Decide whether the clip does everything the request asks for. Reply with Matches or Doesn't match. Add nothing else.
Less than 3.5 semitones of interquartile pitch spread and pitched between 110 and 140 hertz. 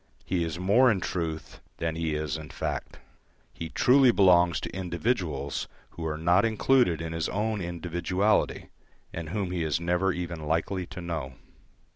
Doesn't match